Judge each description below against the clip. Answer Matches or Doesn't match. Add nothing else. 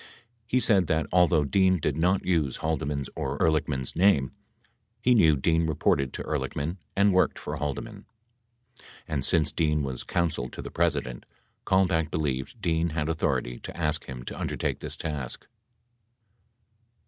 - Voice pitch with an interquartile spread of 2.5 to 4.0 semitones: Matches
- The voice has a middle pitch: Doesn't match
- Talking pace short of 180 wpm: Matches